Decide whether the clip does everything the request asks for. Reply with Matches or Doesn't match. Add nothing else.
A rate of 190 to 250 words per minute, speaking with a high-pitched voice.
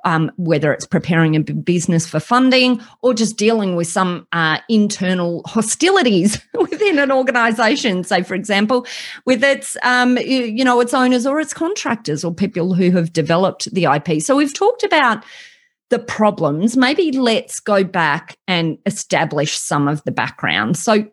Doesn't match